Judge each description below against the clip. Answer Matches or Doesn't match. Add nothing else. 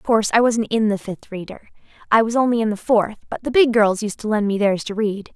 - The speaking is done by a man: Doesn't match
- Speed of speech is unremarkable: Doesn't match